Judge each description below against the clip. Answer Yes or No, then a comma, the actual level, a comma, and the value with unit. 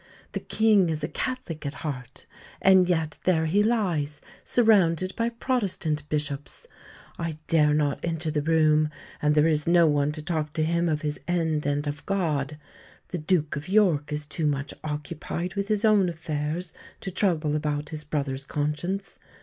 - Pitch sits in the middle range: Yes, medium, 155 Hz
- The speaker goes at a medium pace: Yes, average, 170 wpm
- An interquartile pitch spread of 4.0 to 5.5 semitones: No, average, 3.3 semitones